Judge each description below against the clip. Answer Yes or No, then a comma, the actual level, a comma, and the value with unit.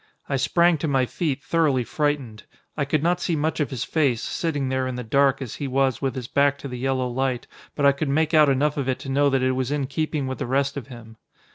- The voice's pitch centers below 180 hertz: Yes, low, 135 Hz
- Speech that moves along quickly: Yes, fast, 260 wpm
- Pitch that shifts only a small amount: Yes, narrow, 2.2 semitones